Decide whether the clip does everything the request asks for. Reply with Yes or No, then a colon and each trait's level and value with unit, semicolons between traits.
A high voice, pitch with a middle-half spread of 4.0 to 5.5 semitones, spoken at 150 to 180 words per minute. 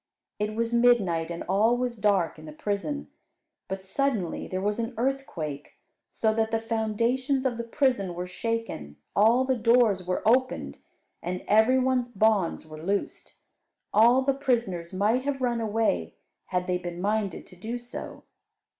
Yes: high, 220 Hz; average, 4.6 semitones; average, 160 wpm